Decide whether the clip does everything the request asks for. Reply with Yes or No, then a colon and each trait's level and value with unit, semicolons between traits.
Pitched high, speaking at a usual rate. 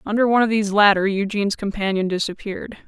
Yes: high, 205 Hz; average, 165 wpm